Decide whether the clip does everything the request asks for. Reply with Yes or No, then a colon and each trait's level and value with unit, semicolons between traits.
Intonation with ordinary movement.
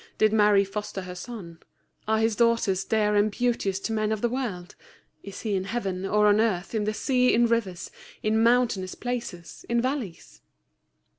Yes: average, 3.2 semitones